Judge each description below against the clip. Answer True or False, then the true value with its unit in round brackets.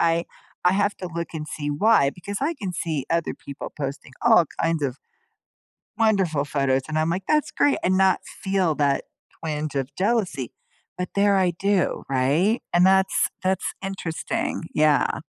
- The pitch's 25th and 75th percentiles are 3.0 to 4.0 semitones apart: False (4.6 semitones)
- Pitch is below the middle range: False (170 Hz)